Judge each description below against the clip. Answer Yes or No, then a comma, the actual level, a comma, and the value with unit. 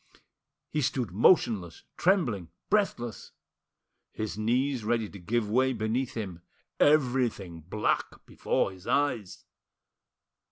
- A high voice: No, low, 115 Hz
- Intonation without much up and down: No, average, 4.5 semitones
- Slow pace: Yes, slow, 105 wpm